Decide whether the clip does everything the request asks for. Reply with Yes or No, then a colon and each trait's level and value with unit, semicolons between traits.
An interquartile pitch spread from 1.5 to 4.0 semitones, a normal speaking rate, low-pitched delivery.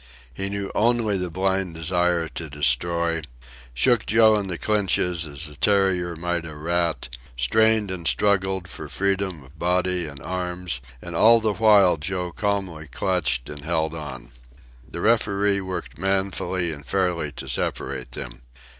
Yes: average, 3.4 semitones; average, 150 wpm; very low, 90 Hz